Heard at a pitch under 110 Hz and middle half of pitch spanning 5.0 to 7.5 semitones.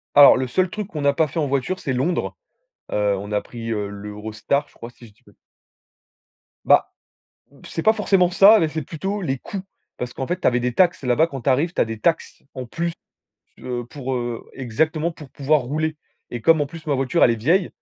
No: medium, 140 Hz; average, 5.3 semitones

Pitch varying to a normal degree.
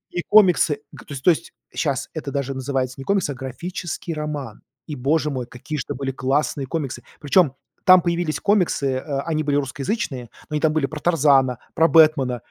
Yes: average, 3.4 semitones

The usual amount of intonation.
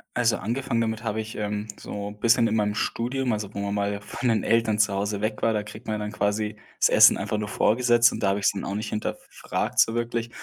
No: narrow, 2.0 semitones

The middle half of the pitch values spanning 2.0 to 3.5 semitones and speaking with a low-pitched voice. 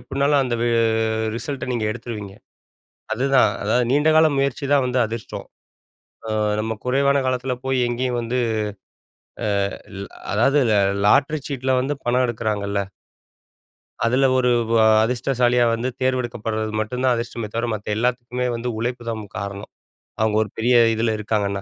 Yes: average, 2.8 semitones; low, 120 Hz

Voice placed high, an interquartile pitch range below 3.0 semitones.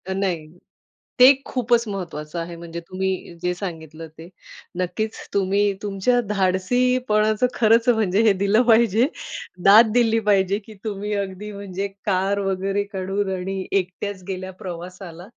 Yes: high, 195 Hz; narrow, 2.6 semitones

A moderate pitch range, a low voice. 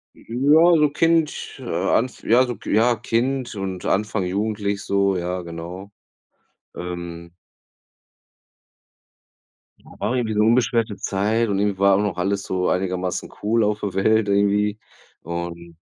Yes: average, 3.8 semitones; low, 100 Hz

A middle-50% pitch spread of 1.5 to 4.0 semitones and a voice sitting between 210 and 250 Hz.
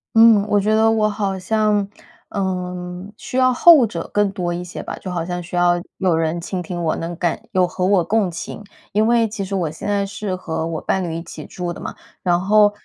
No: average, 3.1 semitones; medium, 185 Hz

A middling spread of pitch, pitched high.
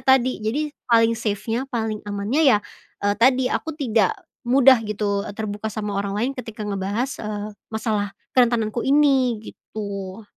Yes: average, 3.5 semitones; high, 220 Hz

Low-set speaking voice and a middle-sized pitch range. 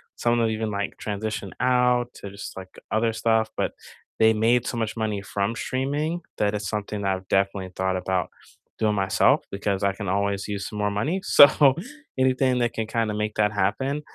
Yes: low, 105 Hz; average, 3.0 semitones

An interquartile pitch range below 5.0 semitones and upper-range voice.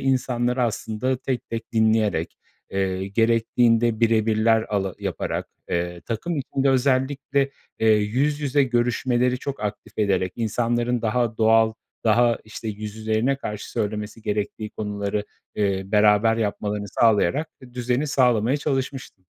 No: average, 2.9 semitones; low, 115 Hz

